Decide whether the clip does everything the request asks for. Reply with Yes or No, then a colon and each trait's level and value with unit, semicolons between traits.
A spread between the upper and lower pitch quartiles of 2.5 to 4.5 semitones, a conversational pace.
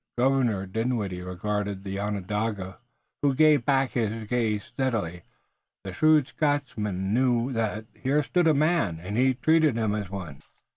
No: average, 5.1 semitones; average, 145 wpm